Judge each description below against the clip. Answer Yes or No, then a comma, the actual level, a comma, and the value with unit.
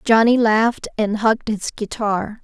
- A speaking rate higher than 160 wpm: No, average, 150 wpm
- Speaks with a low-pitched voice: No, high, 215 Hz